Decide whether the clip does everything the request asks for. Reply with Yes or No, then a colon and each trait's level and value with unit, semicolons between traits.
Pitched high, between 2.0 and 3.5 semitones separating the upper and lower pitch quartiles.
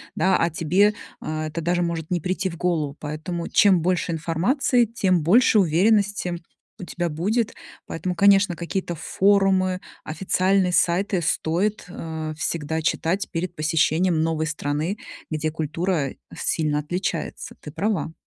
No: medium, 175 Hz; average, 3.2 semitones